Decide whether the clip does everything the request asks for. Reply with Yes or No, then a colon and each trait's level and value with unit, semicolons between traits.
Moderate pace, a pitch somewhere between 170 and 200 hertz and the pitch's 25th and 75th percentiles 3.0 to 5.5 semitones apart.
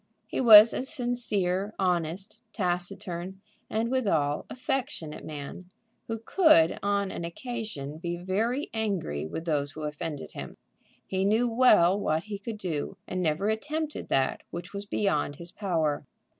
Yes: average, 145 wpm; high, 190 Hz; average, 5.2 semitones